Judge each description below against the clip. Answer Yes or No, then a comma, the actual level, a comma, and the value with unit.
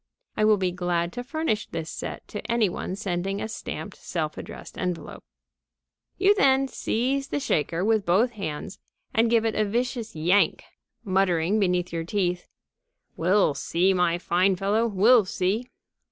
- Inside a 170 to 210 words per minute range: No, average, 155 wpm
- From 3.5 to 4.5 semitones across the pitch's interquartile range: Yes, average, 4.2 semitones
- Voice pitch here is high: Yes, high, 195 Hz